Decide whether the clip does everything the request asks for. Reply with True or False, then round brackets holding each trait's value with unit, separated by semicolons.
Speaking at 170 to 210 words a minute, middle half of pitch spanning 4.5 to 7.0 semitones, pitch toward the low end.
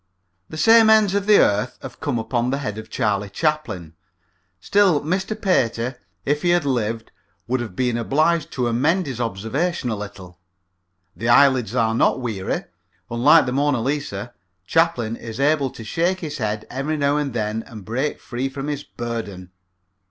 True (175 wpm; 5.2 semitones; 125 Hz)